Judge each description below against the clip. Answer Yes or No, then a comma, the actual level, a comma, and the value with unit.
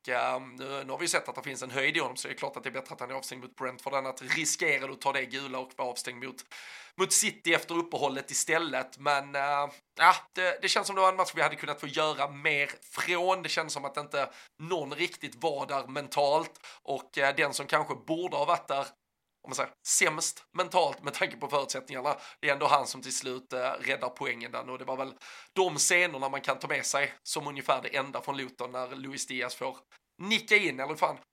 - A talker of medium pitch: Yes, medium, 145 Hz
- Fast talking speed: Yes, fast, 240 wpm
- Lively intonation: No, average, 4.0 semitones